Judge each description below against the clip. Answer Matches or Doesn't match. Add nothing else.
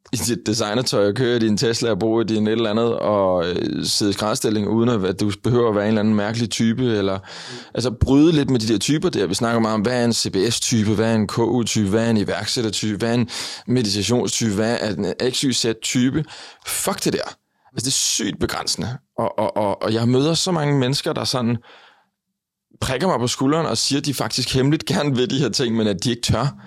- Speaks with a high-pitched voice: Doesn't match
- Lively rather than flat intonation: Doesn't match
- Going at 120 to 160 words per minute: Doesn't match